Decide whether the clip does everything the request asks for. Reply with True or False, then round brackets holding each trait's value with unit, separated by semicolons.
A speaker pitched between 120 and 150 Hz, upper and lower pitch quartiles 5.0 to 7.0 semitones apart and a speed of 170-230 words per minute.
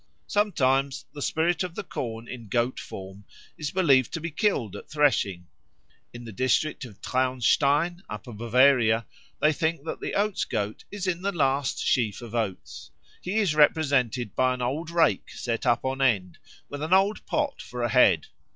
True (135 Hz; 5.5 semitones; 175 wpm)